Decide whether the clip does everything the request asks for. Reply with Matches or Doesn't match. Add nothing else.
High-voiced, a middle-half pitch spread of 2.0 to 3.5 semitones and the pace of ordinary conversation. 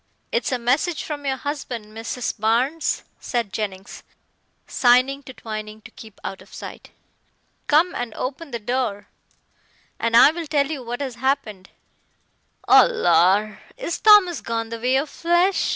Doesn't match